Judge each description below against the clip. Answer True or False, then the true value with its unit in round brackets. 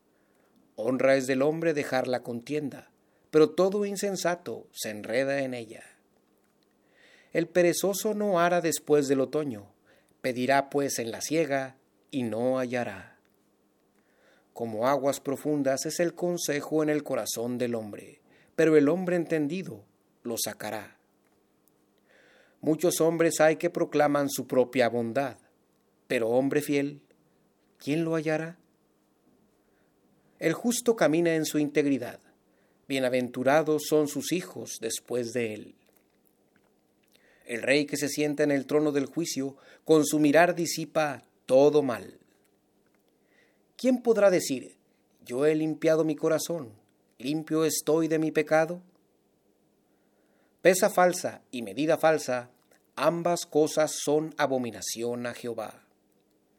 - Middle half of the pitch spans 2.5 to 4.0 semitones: False (4.4 semitones)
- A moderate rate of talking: False (120 wpm)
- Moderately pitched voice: True (145 Hz)